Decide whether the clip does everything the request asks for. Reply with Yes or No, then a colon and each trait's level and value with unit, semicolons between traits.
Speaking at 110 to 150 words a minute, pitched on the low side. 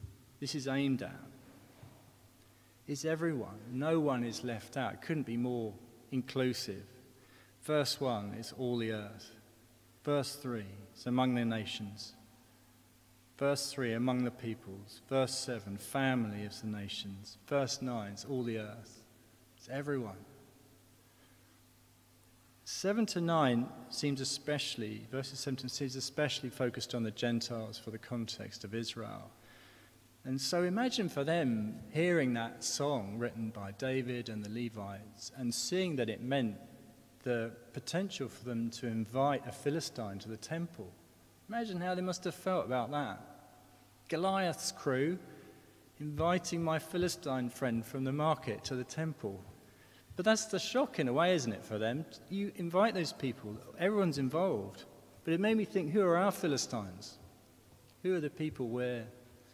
Yes: average, 145 wpm; low, 125 Hz